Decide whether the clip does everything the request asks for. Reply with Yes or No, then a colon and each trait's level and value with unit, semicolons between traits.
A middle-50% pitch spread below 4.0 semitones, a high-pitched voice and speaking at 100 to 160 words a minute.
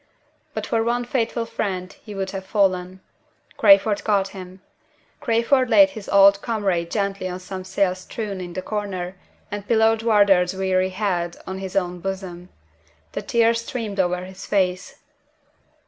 Yes: average, 2.8 semitones; high, 195 Hz; average, 150 wpm